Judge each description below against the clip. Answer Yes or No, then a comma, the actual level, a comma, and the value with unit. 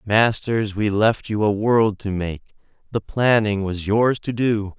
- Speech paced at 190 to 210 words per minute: No, average, 175 wpm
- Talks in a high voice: No, low, 105 Hz